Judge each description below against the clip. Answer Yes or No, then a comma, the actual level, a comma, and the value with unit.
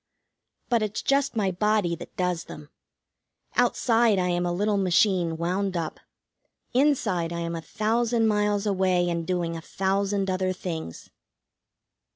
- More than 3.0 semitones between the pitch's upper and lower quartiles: Yes, average, 3.4 semitones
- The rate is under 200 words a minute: Yes, average, 145 wpm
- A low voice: No, high, 190 Hz